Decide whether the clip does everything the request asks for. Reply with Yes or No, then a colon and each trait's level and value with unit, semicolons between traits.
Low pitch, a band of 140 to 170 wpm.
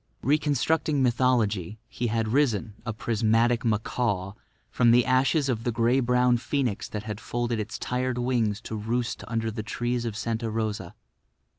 Yes: low, 115 Hz; average, 155 wpm